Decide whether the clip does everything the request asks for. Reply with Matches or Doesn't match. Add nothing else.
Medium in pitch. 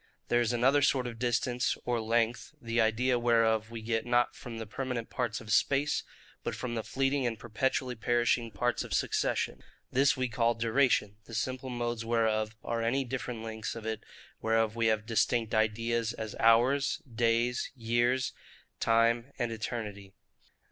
Doesn't match